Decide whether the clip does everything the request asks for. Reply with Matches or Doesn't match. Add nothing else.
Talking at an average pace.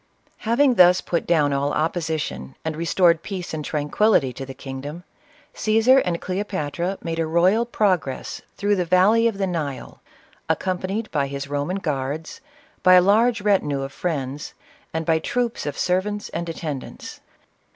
Matches